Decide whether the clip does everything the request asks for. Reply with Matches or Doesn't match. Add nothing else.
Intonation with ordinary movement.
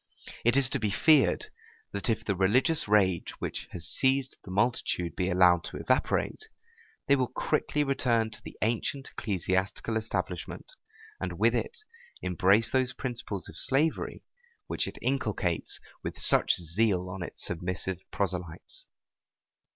Doesn't match